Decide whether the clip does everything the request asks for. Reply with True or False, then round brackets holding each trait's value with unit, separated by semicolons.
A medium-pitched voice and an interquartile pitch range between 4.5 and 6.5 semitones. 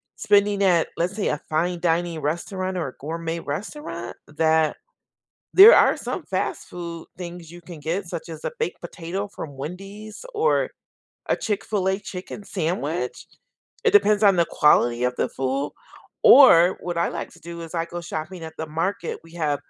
False (170 Hz; 3.2 semitones)